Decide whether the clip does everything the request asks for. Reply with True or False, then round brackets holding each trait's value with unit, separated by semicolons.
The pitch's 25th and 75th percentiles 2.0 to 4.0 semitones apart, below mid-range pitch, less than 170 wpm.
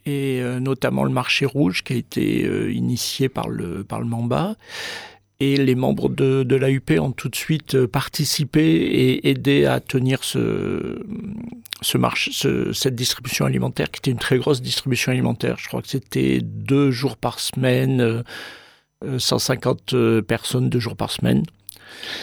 True (3.1 semitones; 130 Hz; 155 wpm)